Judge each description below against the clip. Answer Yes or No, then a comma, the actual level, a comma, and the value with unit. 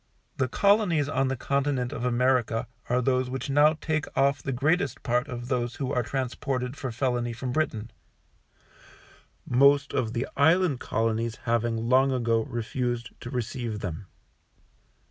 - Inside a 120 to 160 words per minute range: Yes, average, 145 wpm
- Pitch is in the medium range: No, low, 125 Hz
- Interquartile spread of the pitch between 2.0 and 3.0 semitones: Yes, average, 2.7 semitones